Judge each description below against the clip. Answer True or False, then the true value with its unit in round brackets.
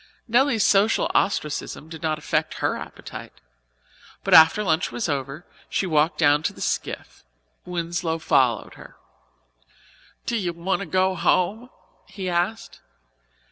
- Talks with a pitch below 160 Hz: False (175 Hz)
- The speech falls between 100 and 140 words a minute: True (135 wpm)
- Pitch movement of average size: True (3.8 semitones)